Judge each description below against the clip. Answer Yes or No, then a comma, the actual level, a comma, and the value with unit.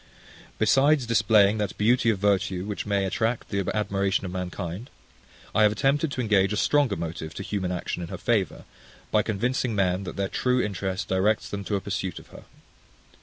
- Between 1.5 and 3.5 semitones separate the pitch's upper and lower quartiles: Yes, average, 2.9 semitones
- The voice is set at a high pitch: No, low, 100 Hz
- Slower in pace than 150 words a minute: No, average, 185 wpm